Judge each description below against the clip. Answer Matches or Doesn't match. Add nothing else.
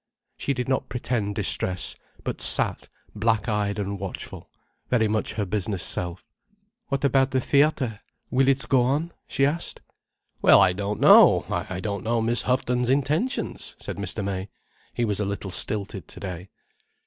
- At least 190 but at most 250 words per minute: Doesn't match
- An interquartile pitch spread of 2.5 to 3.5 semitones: Doesn't match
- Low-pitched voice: Matches